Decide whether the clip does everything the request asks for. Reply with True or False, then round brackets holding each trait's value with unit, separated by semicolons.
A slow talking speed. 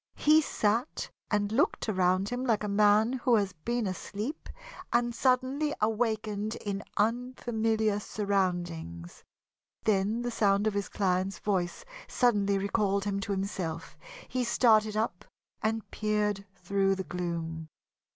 True (130 wpm)